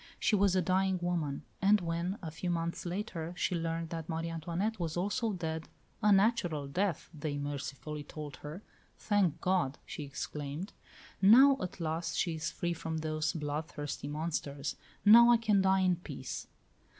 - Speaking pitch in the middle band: Yes, medium, 170 Hz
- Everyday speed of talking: Yes, average, 160 wpm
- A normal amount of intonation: Yes, average, 3.6 semitones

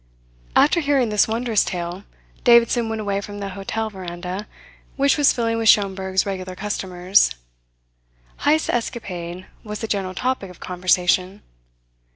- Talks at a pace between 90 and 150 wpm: Yes, slow, 135 wpm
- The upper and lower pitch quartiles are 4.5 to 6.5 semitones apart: No, average, 3.7 semitones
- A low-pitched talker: No, high, 200 Hz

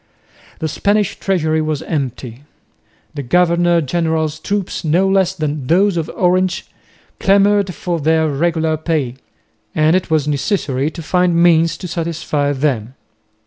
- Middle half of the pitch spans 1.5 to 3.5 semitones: Yes, average, 3.0 semitones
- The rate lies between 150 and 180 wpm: No, slow, 135 wpm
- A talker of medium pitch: Yes, medium, 160 Hz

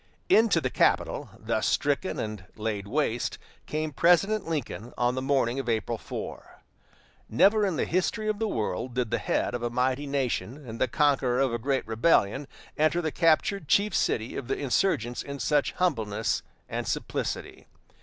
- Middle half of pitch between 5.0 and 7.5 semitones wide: Yes, wide, 5.5 semitones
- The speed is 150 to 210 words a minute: Yes, average, 170 wpm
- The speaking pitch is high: No, low, 135 Hz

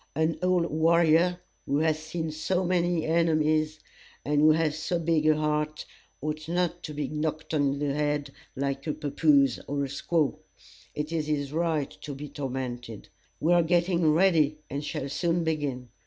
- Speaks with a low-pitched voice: No, medium, 155 Hz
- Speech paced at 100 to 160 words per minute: No, average, 170 wpm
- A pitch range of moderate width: No, narrow, 2.3 semitones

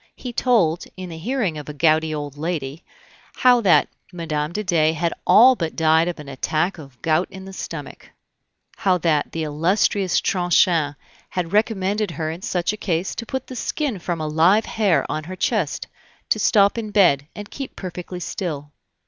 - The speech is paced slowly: No, average, 180 wpm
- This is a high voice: No, medium, 175 Hz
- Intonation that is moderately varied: Yes, average, 4.5 semitones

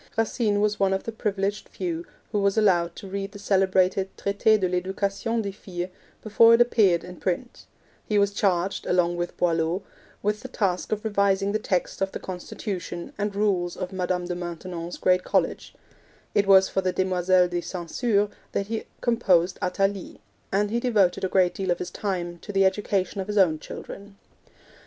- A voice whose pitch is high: Yes, high, 195 Hz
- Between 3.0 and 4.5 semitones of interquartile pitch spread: No, narrow, 2.4 semitones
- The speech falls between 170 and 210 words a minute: Yes, average, 185 wpm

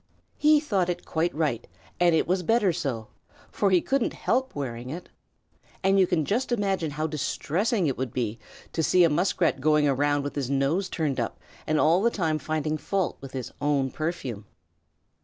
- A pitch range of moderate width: Yes, average, 5.0 semitones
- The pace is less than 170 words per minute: No, average, 185 wpm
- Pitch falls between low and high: Yes, medium, 155 Hz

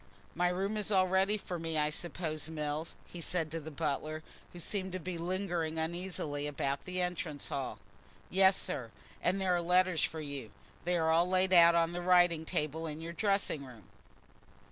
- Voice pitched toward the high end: No, medium, 170 Hz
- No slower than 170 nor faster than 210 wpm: Yes, average, 185 wpm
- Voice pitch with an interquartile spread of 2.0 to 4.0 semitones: Yes, average, 2.8 semitones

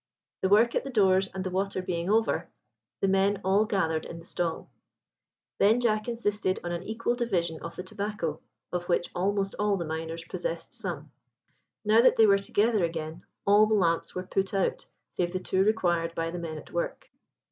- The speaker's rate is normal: Yes, average, 190 wpm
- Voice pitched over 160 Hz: Yes, high, 190 Hz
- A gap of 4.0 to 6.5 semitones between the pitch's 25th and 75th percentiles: No, average, 3.6 semitones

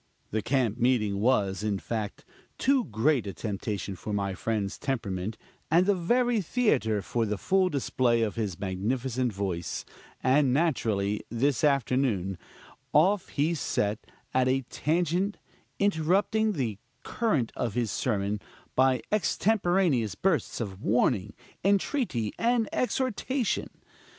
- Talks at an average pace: No, slow, 125 wpm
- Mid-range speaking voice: No, low, 125 Hz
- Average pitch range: No, wide, 8.9 semitones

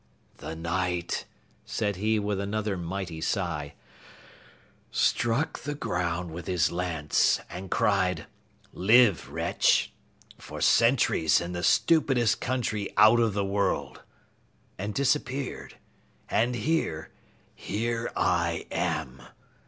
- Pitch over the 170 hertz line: No, low, 100 Hz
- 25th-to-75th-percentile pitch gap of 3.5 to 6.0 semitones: Yes, average, 5.0 semitones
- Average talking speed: No, slow, 105 wpm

